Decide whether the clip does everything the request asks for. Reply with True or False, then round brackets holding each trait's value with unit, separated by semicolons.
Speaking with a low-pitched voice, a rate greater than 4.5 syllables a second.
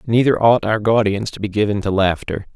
True (110 Hz; 5.5 syllables/s)